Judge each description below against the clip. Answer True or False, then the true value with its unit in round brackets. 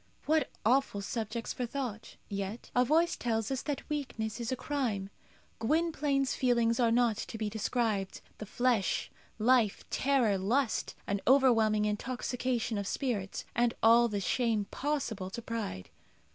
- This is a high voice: True (235 Hz)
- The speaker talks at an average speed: True (145 wpm)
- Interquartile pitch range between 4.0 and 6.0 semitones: False (3.4 semitones)